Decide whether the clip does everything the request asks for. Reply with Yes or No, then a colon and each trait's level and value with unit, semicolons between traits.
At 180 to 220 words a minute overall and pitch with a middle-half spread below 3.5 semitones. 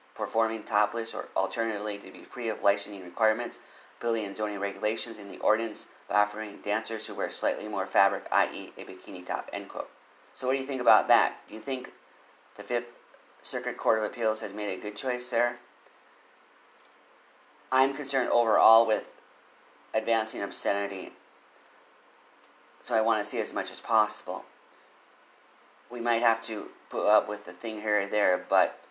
No: average, 170 wpm; narrow, 2.5 semitones